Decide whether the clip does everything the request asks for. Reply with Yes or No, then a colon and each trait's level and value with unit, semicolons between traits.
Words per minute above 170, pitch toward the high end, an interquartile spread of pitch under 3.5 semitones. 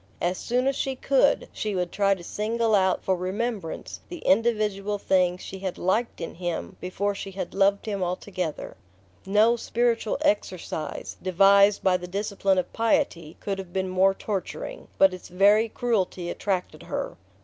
No: average, 160 wpm; high, 195 Hz; average, 2.8 semitones